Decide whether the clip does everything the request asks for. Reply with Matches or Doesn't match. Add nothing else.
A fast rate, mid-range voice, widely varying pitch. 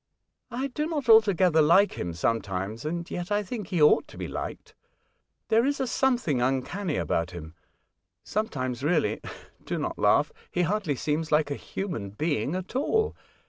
Doesn't match